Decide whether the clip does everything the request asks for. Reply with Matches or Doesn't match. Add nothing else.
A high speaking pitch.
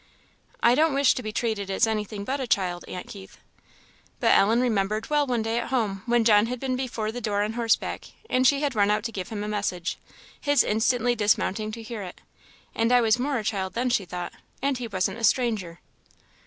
Matches